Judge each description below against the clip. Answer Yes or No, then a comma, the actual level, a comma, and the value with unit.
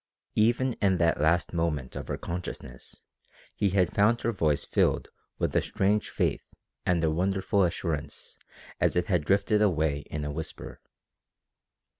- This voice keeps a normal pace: Yes, average, 150 wpm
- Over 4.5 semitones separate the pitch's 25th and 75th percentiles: No, average, 4.1 semitones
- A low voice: Yes, very low, 90 Hz